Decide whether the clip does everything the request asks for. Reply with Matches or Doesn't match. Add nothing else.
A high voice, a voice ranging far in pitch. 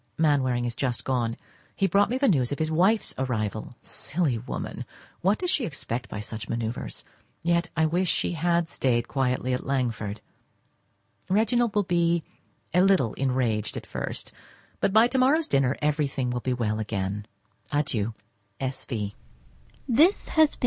Doesn't match